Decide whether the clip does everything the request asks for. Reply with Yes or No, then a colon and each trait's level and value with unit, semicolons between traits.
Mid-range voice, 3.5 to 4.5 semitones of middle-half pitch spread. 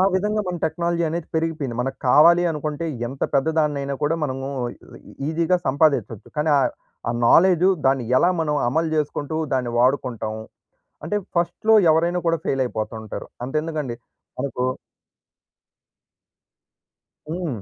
Yes: medium, 150 Hz; average, 4.0 semitones